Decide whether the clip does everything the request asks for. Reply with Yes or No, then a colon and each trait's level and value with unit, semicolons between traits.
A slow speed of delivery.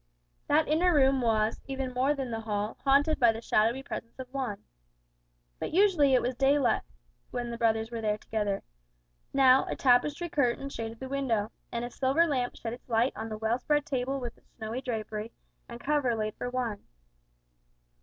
No: average, 185 wpm